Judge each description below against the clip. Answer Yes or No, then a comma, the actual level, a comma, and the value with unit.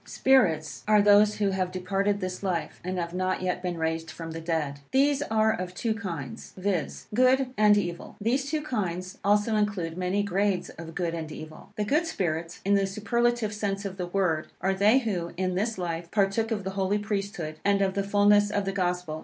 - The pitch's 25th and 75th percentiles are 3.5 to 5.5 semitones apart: No, average, 3.0 semitones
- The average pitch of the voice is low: No, high, 195 Hz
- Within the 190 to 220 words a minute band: Yes, fast, 205 wpm